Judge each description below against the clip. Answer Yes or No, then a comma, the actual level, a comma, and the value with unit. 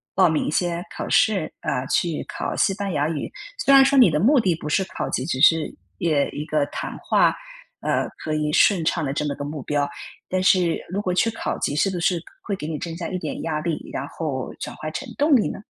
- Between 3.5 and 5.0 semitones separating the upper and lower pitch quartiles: Yes, average, 4.0 semitones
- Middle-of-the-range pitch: Yes, medium, 165 Hz